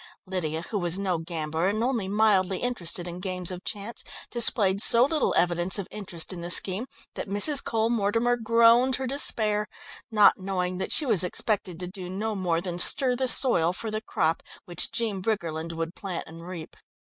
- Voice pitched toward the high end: Yes, high, 195 Hz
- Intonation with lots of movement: No, average, 4.3 semitones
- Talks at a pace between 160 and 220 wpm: Yes, average, 185 wpm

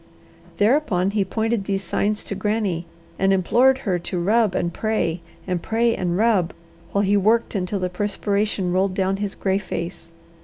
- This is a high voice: Yes, high, 195 Hz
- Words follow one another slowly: No, average, 165 wpm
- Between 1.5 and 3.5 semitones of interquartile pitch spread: Yes, average, 2.8 semitones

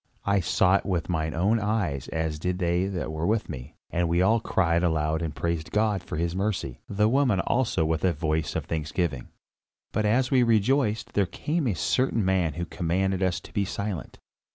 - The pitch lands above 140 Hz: No, very low, 90 Hz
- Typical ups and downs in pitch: Yes, average, 4.4 semitones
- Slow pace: No, average, 200 wpm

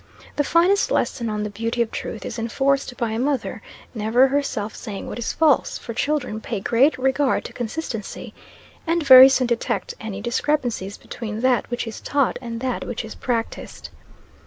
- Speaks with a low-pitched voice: No, high, 240 Hz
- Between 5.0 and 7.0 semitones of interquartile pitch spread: No, average, 3.4 semitones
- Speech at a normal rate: Yes, average, 175 wpm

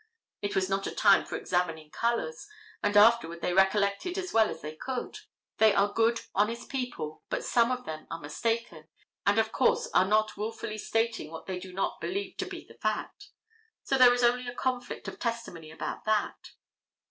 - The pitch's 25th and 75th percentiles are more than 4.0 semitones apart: Yes, average, 4.4 semitones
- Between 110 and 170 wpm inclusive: No, average, 190 wpm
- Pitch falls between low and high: No, high, 215 Hz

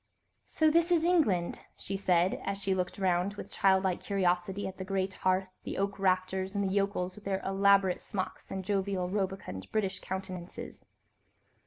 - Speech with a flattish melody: Yes, narrow, 1.3 semitones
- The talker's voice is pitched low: No, high, 190 Hz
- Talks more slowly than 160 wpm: No, average, 170 wpm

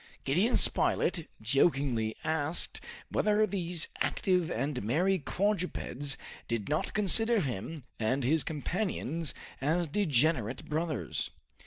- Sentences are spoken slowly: Yes, slow, 105 wpm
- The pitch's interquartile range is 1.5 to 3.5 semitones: No, average, 5.2 semitones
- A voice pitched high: No, medium, 155 Hz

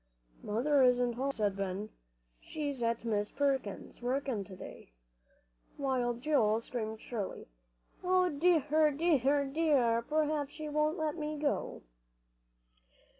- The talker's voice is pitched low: No, very high, 270 Hz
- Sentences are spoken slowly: Yes, slow, 120 wpm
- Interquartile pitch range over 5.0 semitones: No, average, 4.6 semitones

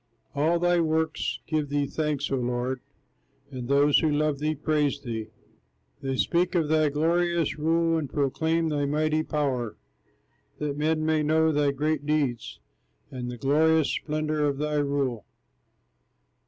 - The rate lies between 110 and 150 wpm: Yes, average, 145 wpm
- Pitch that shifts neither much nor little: No, narrow, 2.0 semitones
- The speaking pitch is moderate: Yes, medium, 150 Hz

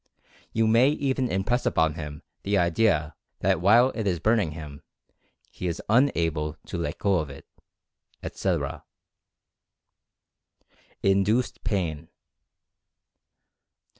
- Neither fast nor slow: No, slow, 110 wpm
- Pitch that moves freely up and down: Yes, wide, 6.1 semitones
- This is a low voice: Yes, very low, 95 Hz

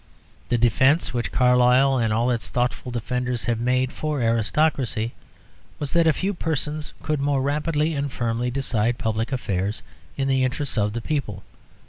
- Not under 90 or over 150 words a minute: No, average, 160 wpm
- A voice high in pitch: No, low, 125 Hz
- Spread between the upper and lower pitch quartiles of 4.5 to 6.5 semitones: No, average, 3.4 semitones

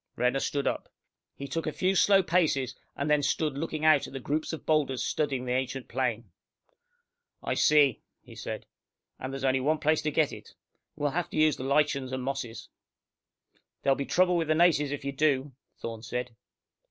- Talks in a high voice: No, medium, 140 Hz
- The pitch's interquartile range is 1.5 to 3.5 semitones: Yes, average, 2.8 semitones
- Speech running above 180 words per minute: Yes, average, 195 wpm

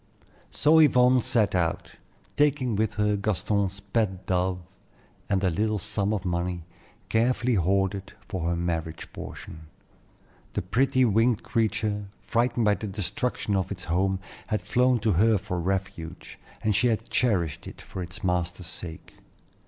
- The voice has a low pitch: Yes, low, 100 Hz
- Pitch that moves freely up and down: No, average, 3.8 semitones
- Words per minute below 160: Yes, average, 145 wpm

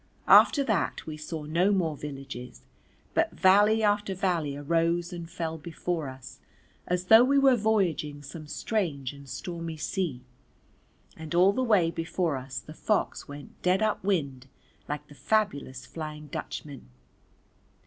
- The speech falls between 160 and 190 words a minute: No, average, 145 wpm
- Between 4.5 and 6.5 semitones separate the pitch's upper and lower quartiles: Yes, average, 4.8 semitones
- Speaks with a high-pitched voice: No, medium, 165 Hz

